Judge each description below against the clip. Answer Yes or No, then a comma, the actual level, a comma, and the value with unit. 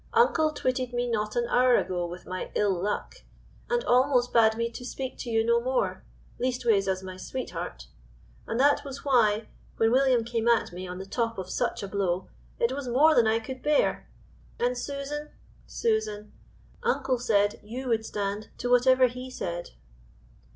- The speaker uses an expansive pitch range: No, average, 3.7 semitones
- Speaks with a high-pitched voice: Yes, high, 235 Hz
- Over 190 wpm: No, average, 175 wpm